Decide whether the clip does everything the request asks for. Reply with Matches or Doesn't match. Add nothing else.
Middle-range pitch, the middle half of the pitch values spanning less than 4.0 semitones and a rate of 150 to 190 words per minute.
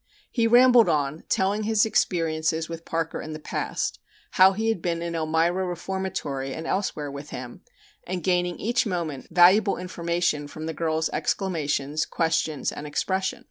Matches